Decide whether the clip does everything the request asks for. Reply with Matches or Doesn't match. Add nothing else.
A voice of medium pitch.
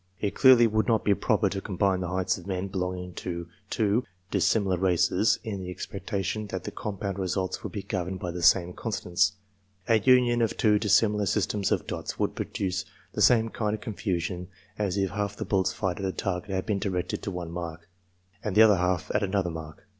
Doesn't match